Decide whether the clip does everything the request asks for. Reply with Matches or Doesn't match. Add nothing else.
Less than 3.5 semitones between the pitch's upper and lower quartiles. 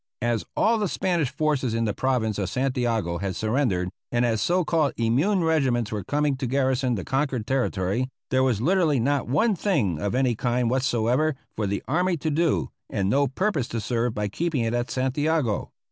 Doesn't match